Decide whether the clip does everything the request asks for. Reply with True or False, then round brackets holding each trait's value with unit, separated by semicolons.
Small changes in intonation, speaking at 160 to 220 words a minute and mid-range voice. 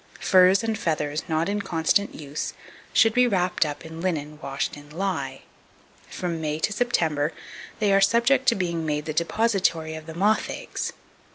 False (4.6 semitones; 170 wpm; 170 Hz)